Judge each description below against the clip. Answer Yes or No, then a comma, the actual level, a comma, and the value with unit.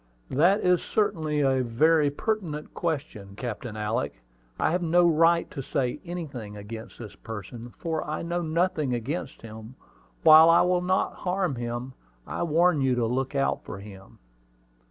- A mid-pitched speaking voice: Yes, medium, 145 Hz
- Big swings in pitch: Yes, wide, 6.2 semitones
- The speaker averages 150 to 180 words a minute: Yes, average, 155 wpm